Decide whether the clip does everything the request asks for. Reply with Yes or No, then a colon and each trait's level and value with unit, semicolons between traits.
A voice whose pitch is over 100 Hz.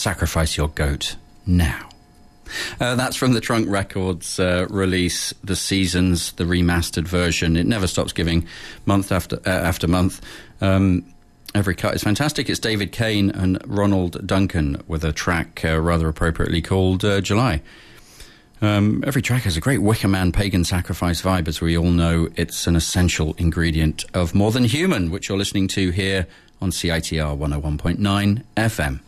No: very low, 90 Hz